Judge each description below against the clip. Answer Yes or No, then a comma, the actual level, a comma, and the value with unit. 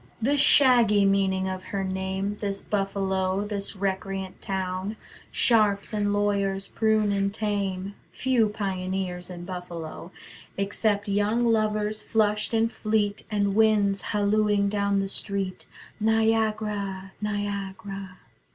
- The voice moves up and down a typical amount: No, narrow, 1.7 semitones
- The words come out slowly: Yes, slow, 115 wpm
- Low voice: No, high, 200 Hz